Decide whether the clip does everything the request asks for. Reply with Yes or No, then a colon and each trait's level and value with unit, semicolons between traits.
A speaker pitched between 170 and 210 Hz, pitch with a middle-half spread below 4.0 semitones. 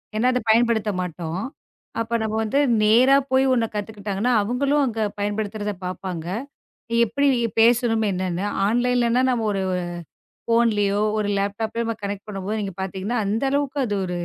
No: high, 220 Hz; average, 2.9 semitones